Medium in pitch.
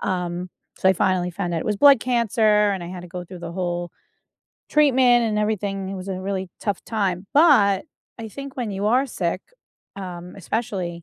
No: high, 195 Hz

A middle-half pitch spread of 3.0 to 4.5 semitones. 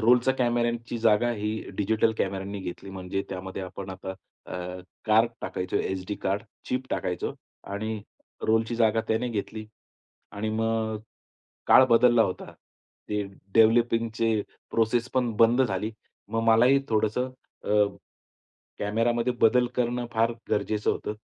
No: narrow, 2.4 semitones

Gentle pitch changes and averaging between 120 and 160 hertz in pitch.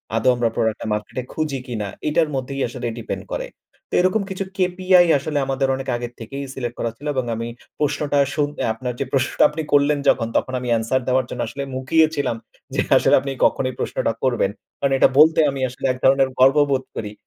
No: average, 3.2 semitones; low, 135 Hz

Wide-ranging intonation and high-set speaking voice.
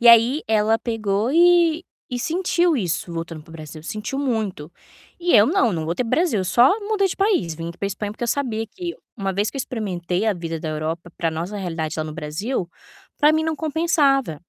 Yes: wide, 9.0 semitones; high, 215 Hz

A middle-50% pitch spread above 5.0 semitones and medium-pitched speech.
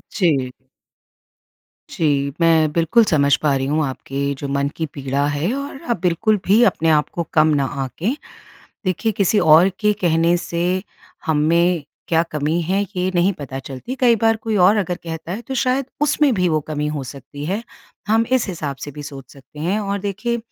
Yes: wide, 5.6 semitones; medium, 170 Hz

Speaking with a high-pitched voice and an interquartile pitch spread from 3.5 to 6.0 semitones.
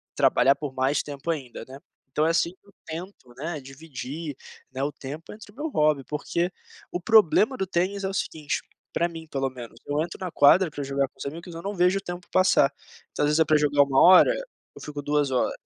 No: medium, 155 Hz; average, 4.4 semitones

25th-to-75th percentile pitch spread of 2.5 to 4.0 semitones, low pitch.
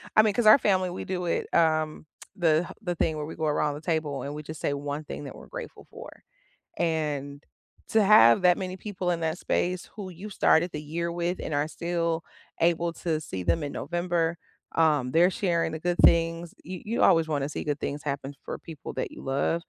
No: average, 2.8 semitones; medium, 165 Hz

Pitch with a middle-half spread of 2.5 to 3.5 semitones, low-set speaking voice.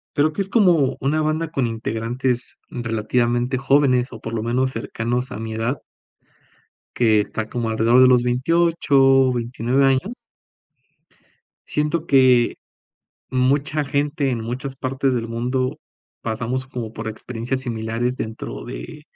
Yes: average, 2.8 semitones; low, 125 Hz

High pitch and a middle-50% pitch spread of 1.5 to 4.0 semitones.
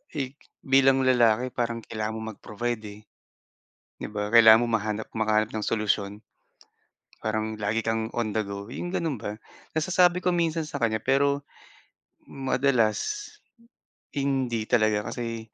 No: low, 115 Hz; average, 3.7 semitones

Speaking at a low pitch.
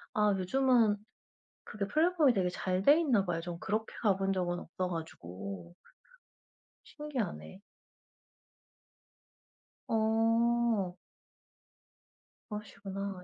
No: high, 200 Hz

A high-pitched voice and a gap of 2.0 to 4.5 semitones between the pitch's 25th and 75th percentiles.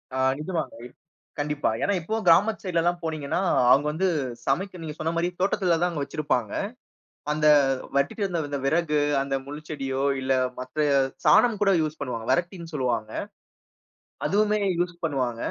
No: medium, 155 Hz; average, 4.2 semitones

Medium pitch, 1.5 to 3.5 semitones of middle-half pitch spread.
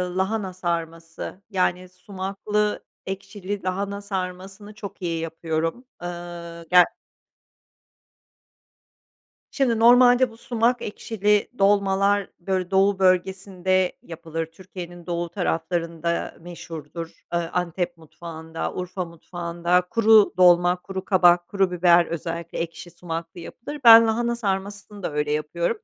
Yes: medium, 180 Hz; average, 2.9 semitones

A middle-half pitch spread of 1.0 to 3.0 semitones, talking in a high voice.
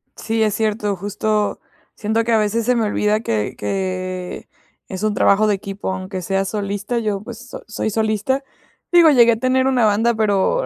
Yes: narrow, 2.6 semitones; high, 215 Hz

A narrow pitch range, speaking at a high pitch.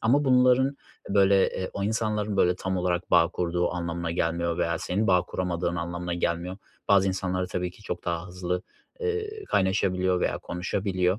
No: narrow, 2.3 semitones; very low, 90 Hz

